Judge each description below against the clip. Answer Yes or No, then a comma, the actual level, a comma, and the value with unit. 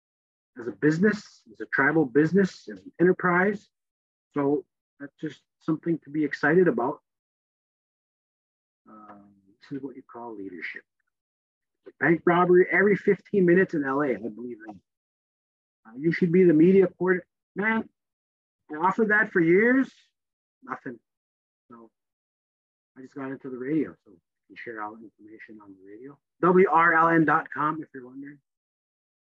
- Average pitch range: No, wide, 7.4 semitones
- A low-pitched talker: No, medium, 150 Hz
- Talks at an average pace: Yes, average, 145 wpm